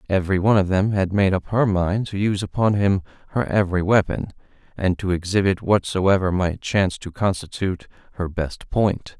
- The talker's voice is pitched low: Yes, very low, 95 Hz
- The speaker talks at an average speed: Yes, average, 175 wpm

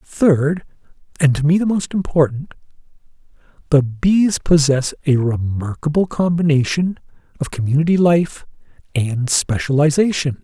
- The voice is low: No, medium, 150 Hz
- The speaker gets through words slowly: Yes, slow, 90 wpm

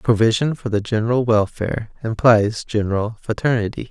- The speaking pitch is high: No, low, 115 Hz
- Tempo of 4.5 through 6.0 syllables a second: Yes, 5.3 syllables/s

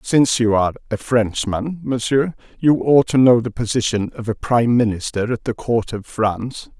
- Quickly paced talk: No, average, 185 wpm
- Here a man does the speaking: Yes, male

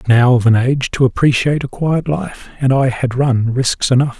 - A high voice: No, low, 130 Hz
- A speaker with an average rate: No, fast, 245 wpm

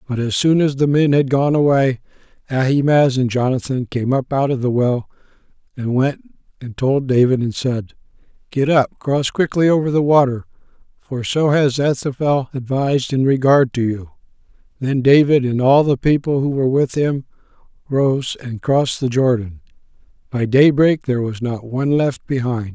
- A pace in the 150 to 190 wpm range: Yes, average, 170 wpm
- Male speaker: Yes, male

